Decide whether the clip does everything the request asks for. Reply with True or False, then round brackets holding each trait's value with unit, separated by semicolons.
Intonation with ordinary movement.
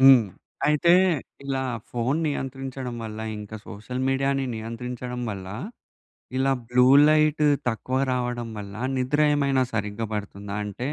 True (3.3 semitones)